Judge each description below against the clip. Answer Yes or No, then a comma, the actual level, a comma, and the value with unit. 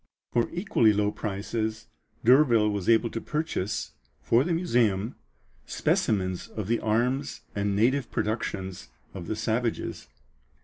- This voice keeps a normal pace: No, slow, 125 wpm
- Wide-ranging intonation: No, average, 3.0 semitones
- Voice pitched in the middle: No, low, 110 Hz